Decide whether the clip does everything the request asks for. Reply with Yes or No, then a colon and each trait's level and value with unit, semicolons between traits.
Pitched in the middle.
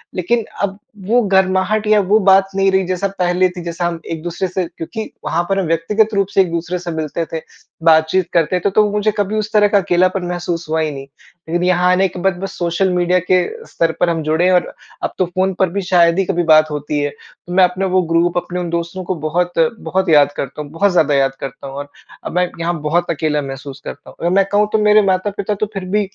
Yes: medium, 180 Hz